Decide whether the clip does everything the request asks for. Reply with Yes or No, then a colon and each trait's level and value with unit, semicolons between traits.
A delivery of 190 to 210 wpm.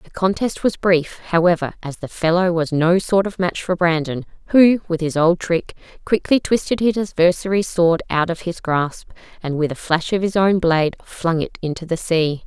Yes: average, 200 wpm